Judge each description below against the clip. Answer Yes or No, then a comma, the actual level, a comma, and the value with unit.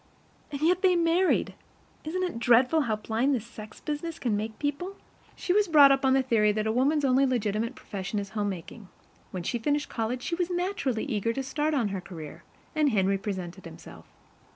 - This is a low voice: No, very high, 250 Hz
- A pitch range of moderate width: No, wide, 6.1 semitones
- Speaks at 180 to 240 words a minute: Yes, average, 195 wpm